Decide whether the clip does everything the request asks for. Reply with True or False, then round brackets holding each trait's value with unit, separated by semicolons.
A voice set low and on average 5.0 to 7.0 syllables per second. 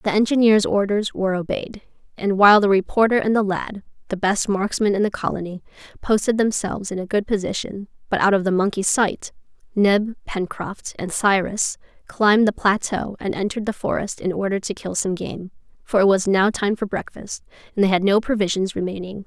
False (200 Hz; 5.4 syllables/s)